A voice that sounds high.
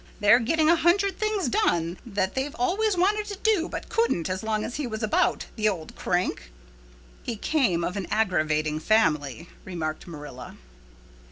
Yes: high, 220 Hz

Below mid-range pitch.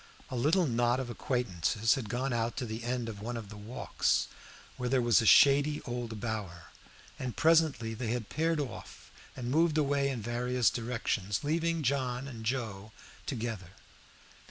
Yes: low, 120 Hz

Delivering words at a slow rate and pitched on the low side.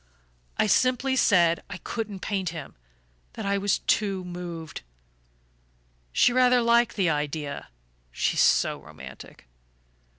No: slow, 120 wpm; high, 195 Hz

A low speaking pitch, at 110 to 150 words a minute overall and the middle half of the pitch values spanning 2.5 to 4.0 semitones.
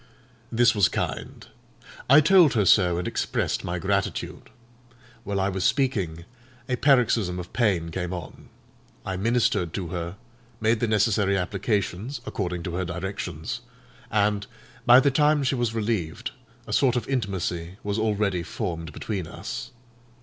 No: low, 100 Hz; average, 145 wpm; average, 4.8 semitones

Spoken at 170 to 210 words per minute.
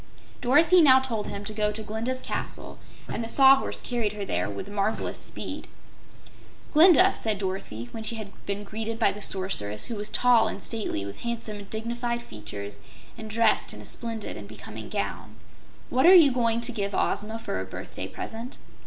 Yes: average, 185 wpm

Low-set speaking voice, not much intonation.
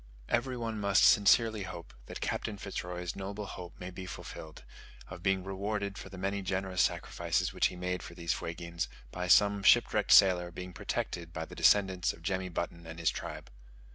Yes: very low, 95 Hz; narrow, 2.2 semitones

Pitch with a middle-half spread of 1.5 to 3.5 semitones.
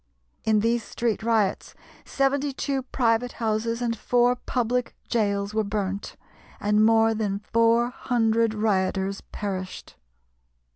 Yes: narrow, 2.5 semitones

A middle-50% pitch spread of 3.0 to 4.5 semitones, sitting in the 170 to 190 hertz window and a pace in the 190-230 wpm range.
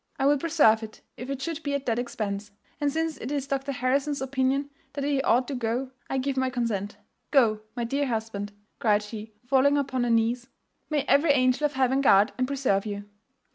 No: average, 3.8 semitones; very high, 260 Hz; fast, 205 wpm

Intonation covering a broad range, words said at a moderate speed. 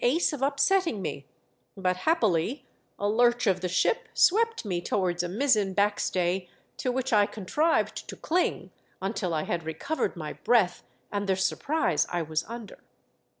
Yes: wide, 6.7 semitones; average, 160 wpm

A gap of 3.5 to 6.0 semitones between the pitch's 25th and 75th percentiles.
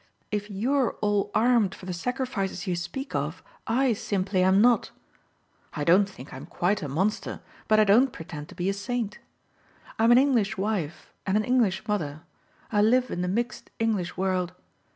Yes: average, 4.0 semitones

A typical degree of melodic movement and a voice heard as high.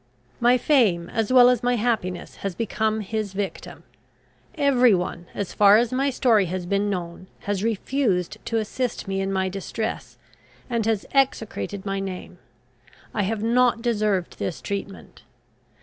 Yes: average, 3.7 semitones; high, 210 Hz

